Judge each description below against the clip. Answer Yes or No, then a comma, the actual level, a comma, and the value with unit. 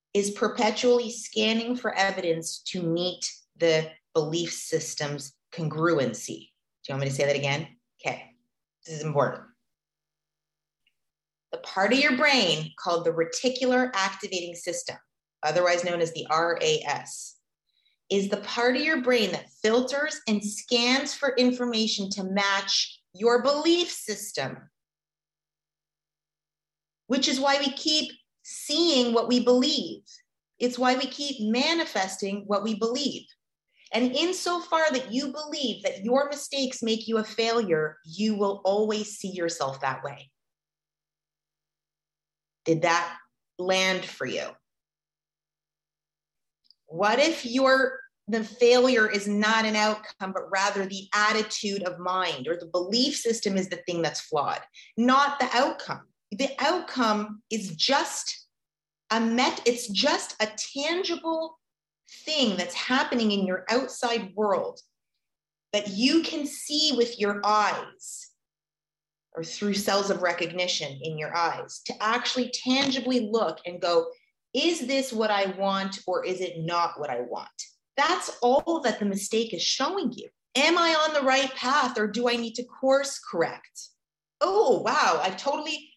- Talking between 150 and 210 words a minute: No, average, 140 wpm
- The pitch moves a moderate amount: No, wide, 6.7 semitones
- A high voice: Yes, high, 215 Hz